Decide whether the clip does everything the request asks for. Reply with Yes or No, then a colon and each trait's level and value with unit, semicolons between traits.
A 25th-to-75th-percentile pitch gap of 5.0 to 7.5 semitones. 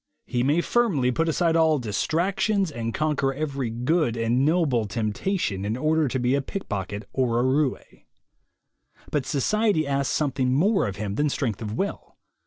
Yes: average, 5.3 semitones